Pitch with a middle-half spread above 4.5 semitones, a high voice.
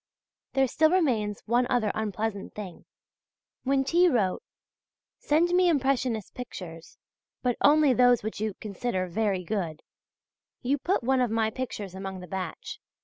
Yes: average, 5.2 semitones; high, 225 Hz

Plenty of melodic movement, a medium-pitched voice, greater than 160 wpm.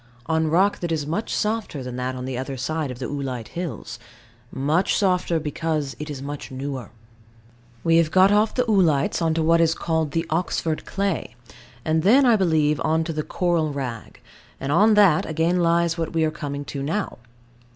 No: average, 3.4 semitones; medium, 160 Hz; average, 195 wpm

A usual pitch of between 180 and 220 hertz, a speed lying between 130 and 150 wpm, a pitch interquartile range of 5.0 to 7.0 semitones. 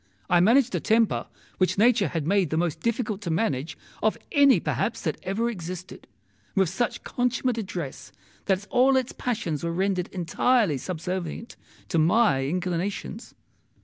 Yes: high, 190 Hz; average, 145 wpm; wide, 5.4 semitones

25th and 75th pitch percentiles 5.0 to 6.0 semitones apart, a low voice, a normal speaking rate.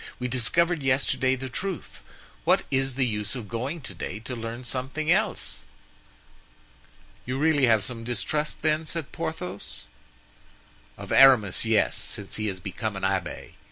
Yes: wide, 5.5 semitones; low, 125 Hz; average, 150 wpm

